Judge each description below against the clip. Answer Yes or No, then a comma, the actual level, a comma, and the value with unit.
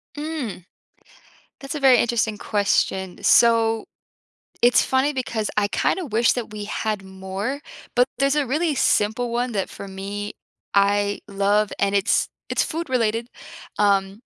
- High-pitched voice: Yes, high, 220 Hz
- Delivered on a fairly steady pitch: No, average, 3.9 semitones